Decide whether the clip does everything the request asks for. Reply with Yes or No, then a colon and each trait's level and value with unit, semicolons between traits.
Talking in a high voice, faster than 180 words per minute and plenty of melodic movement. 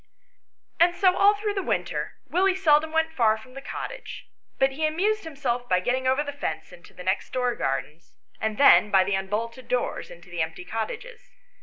Yes: very high, 260 Hz; average, 190 wpm; wide, 8.2 semitones